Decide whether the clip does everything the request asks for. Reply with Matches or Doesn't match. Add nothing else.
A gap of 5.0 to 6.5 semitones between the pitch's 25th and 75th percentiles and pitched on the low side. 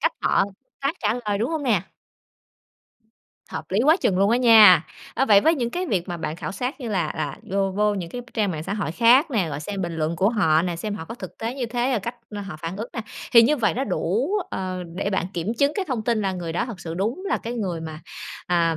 Doesn't match